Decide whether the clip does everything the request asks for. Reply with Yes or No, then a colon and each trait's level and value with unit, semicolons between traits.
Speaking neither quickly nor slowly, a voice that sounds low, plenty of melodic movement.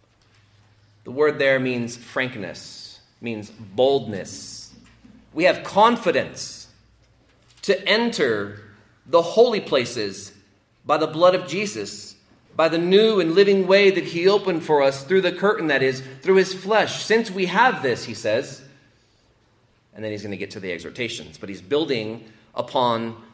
Yes: average, 150 wpm; low, 130 Hz; wide, 8.7 semitones